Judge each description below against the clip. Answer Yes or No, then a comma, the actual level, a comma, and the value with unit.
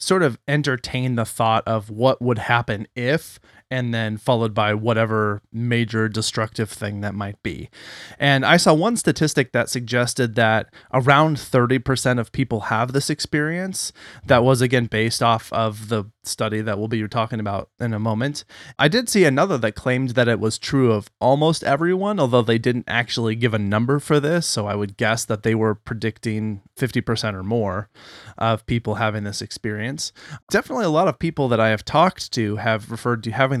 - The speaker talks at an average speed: Yes, average, 185 wpm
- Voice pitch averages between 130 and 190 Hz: No, low, 115 Hz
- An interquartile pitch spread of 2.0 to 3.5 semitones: Yes, average, 3.2 semitones